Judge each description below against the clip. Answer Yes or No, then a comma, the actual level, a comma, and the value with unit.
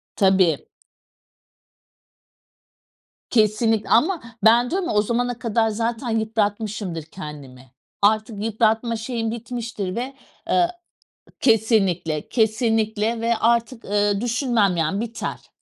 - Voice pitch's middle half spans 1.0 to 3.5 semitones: Yes, narrow, 2.5 semitones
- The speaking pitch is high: Yes, high, 220 Hz